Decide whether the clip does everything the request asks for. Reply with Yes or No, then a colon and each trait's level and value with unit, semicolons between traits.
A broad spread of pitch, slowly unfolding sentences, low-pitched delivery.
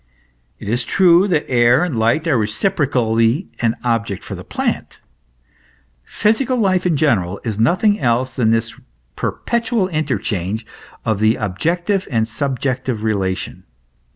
Yes: wide, 7.6 semitones; slow, 130 wpm; low, 125 Hz